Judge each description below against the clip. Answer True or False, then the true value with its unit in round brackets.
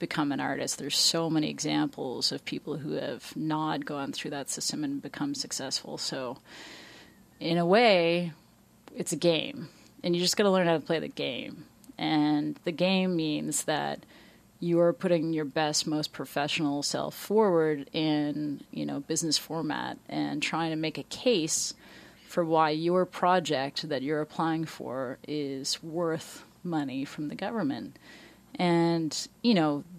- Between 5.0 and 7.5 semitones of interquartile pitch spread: False (2.8 semitones)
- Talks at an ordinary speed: True (155 wpm)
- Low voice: False (160 Hz)